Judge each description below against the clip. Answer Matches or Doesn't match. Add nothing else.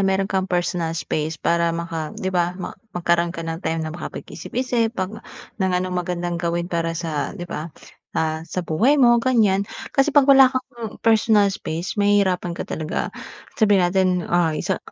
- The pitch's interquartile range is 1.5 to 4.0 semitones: Matches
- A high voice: Doesn't match